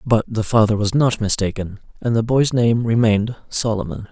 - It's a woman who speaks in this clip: No, male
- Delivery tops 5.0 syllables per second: Yes, 5.2 syllables/s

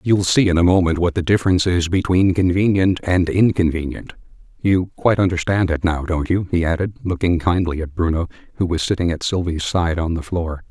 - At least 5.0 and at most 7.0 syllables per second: Yes, 5.6 syllables/s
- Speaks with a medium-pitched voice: No, very low, 90 Hz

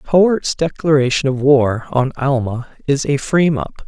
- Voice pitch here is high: No, medium, 140 Hz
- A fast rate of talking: No, average, 155 wpm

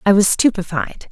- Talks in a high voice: Yes, high, 195 Hz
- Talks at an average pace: Yes, average, 160 wpm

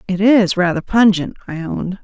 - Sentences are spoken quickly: No, average, 175 wpm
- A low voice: No, high, 190 Hz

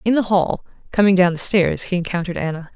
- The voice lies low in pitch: No, medium, 185 Hz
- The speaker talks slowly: No, fast, 215 wpm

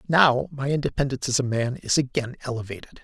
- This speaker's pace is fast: No, average, 180 wpm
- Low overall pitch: Yes, low, 130 Hz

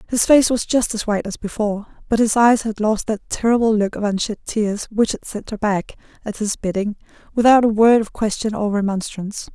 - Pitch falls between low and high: No, high, 215 Hz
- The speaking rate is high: Yes, fast, 215 wpm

